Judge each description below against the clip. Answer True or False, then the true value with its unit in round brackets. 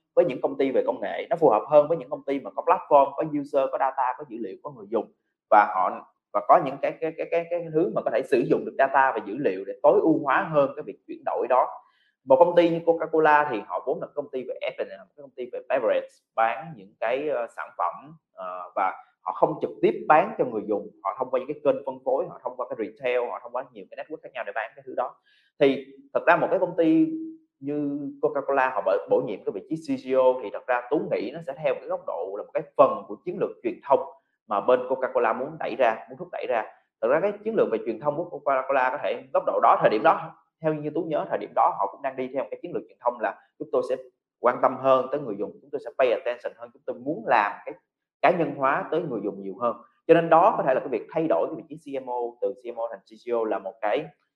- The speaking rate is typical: False (285 wpm)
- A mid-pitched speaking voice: True (155 Hz)